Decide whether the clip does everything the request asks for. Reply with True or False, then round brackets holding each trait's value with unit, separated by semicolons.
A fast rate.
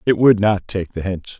True (260 wpm)